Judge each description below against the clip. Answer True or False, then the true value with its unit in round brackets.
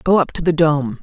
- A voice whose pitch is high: False (160 Hz)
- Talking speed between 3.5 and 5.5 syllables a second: False (6.2 syllables/s)